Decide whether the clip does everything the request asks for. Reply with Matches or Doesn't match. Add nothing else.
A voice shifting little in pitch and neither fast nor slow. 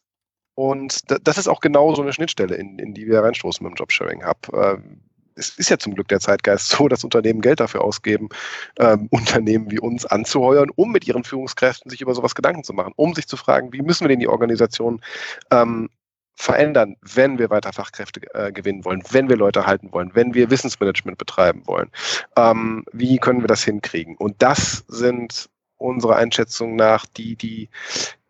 Doesn't match